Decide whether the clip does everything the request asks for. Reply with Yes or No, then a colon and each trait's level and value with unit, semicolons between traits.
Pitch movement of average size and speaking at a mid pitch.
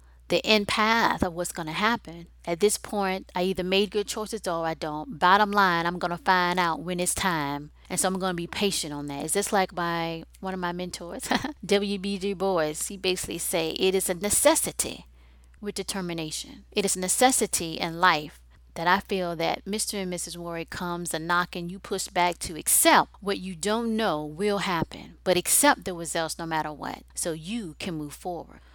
Yes: average, 3.2 semitones; medium, 180 Hz